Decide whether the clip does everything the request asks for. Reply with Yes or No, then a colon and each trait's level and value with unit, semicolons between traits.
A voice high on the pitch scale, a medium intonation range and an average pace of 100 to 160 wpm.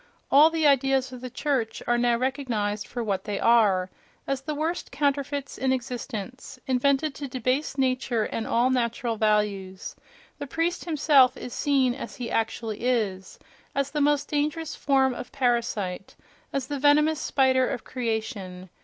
Yes: very high, 255 Hz; average, 3.7 semitones; average, 150 wpm